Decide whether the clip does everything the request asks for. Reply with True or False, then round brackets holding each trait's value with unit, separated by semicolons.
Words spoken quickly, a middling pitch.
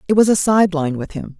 True (260 wpm; 180 Hz)